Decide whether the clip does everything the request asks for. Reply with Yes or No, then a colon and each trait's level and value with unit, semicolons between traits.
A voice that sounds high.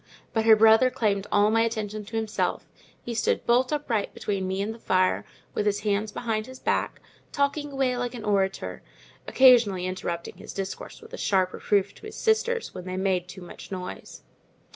Yes: high, 215 Hz